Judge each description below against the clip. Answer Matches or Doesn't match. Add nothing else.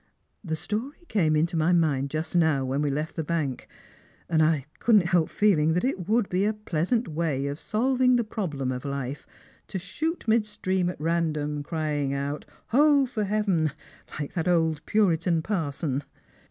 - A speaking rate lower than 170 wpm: Doesn't match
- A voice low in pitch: Doesn't match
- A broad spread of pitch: Matches